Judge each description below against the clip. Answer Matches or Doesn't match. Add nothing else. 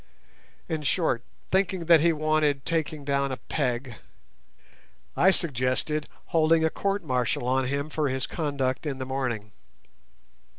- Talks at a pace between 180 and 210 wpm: Doesn't match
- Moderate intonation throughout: Matches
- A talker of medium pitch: Matches